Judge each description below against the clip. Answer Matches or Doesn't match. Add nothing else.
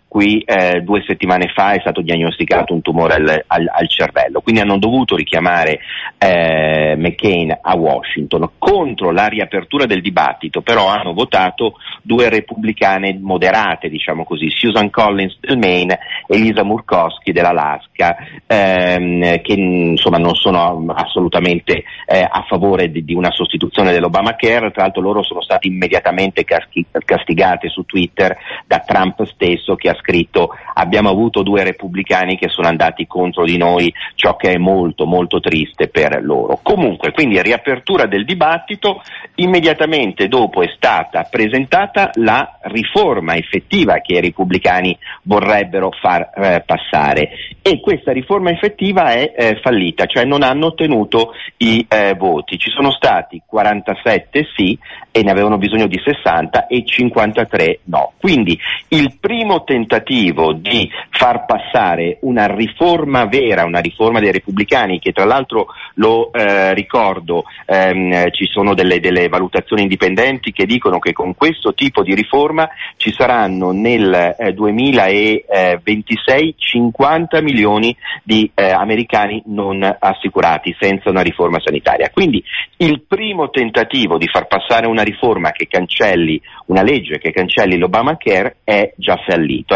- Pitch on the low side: Matches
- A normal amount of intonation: Matches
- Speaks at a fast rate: Doesn't match